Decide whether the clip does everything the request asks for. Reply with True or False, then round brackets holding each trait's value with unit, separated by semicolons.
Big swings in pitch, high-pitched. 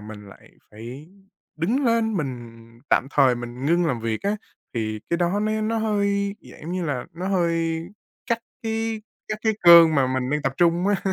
False (8.1 semitones; 170 Hz)